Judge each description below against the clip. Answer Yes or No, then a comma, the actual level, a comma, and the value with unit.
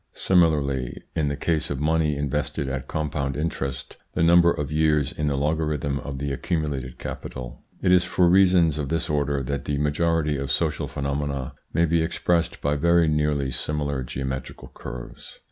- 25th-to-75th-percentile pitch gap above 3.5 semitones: No, average, 2.7 semitones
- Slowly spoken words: No, average, 165 wpm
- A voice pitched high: No, very low, 75 Hz